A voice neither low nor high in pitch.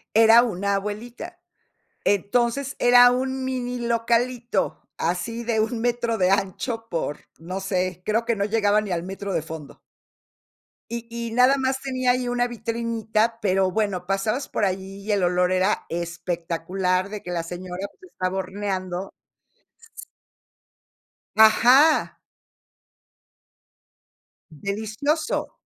No: high, 215 Hz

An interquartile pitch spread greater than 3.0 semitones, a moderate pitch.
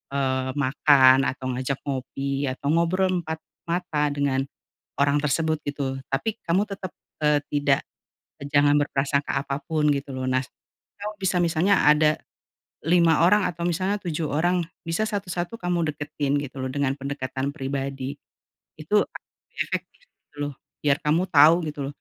Yes: average, 3.6 semitones; medium, 145 Hz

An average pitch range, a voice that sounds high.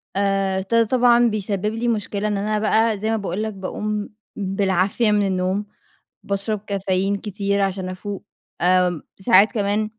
No: narrow, 1.9 semitones; high, 200 Hz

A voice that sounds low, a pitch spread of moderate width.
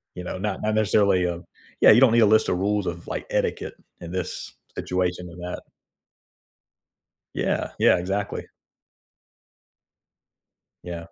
Yes: very low, 90 Hz; average, 3.0 semitones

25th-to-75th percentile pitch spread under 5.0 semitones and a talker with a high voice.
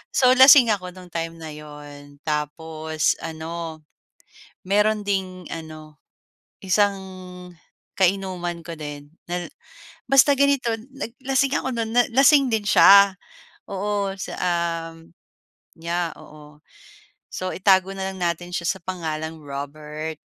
No: average, 4.1 semitones; medium, 175 Hz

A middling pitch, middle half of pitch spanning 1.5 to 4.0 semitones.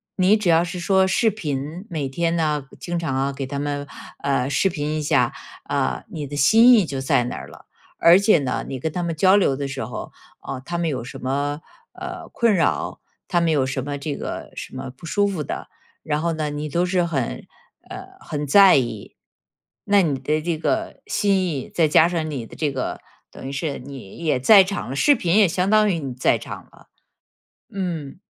No: medium, 155 Hz; average, 4.7 semitones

